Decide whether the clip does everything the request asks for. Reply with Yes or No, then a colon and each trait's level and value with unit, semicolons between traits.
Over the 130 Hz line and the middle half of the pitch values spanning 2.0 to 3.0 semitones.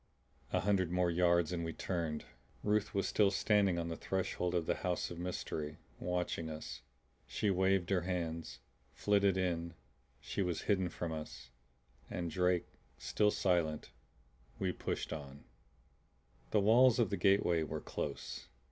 No: very low, 90 Hz; narrow, 2.6 semitones